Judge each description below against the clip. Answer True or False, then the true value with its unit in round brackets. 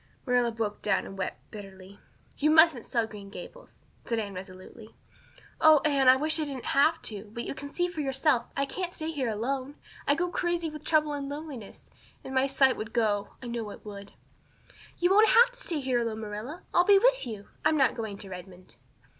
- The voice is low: False (265 Hz)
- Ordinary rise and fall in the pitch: False (6.4 semitones)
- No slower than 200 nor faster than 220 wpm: True (205 wpm)